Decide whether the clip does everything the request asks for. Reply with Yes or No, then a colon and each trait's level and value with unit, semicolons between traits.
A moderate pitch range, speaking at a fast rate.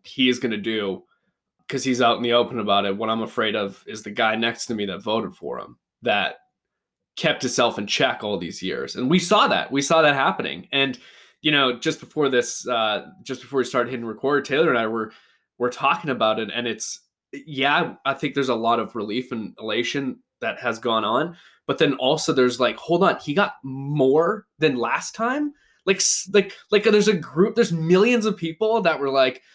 No: wide, 5.8 semitones; fast, 215 wpm